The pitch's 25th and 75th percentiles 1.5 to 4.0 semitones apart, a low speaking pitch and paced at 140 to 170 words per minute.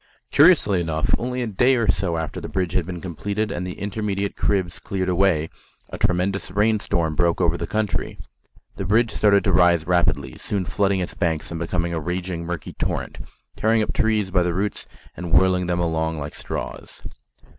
No: average, 3.0 semitones; very low, 90 Hz; average, 190 wpm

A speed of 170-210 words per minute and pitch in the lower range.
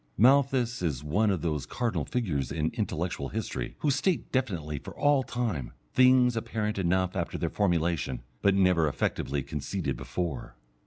No: average, 150 wpm; very low, 95 Hz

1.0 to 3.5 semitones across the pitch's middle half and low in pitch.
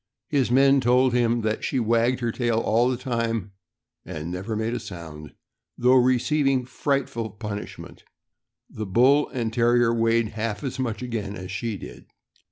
Yes: average, 2.7 semitones; low, 115 Hz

